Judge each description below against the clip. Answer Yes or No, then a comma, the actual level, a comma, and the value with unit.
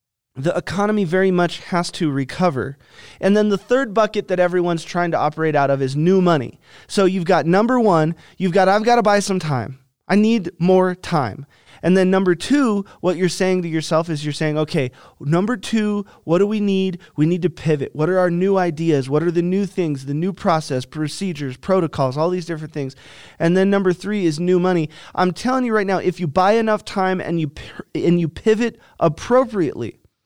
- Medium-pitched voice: Yes, medium, 180 Hz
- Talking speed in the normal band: No, fast, 210 wpm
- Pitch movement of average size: Yes, average, 3.8 semitones